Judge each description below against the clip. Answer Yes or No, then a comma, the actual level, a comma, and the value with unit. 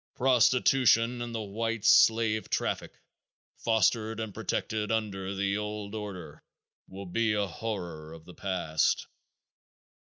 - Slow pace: Yes, slow, 120 wpm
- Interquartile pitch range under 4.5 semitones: Yes, average, 2.8 semitones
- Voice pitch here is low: Yes, low, 105 Hz